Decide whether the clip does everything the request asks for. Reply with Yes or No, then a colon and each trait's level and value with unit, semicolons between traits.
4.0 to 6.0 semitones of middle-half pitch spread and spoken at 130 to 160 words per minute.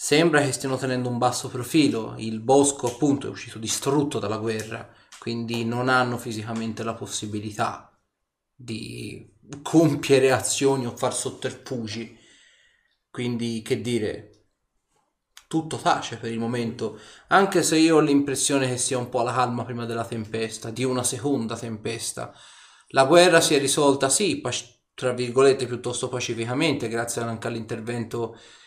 No: average, 2.9 semitones; average, 140 wpm